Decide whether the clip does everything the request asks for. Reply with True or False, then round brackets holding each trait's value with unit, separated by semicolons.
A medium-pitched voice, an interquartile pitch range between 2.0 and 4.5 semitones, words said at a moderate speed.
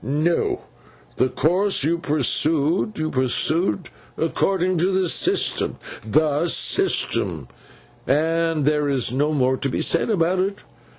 False (155 Hz; 3.7 semitones; 115 wpm)